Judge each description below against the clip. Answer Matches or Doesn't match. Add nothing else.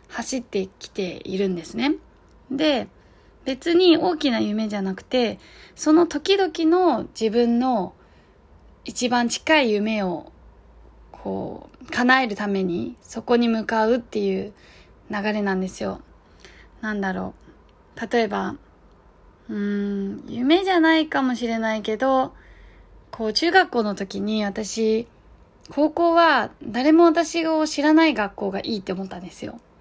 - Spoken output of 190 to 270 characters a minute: Matches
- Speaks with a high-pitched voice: Matches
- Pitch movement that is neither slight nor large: Doesn't match